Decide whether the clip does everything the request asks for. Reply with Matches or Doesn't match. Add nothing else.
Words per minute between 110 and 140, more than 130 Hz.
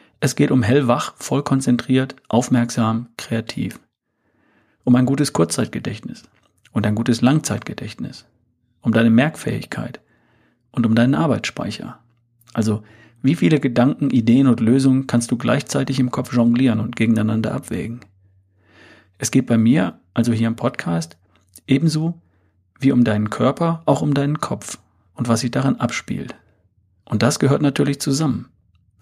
Doesn't match